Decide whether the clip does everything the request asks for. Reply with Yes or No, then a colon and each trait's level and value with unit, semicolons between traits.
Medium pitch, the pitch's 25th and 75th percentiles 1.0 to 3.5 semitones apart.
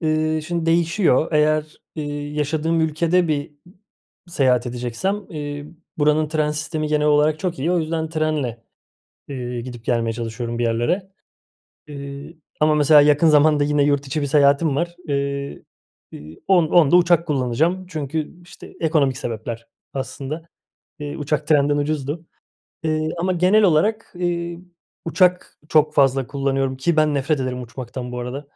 Yes: medium, 150 Hz; average, 3.0 semitones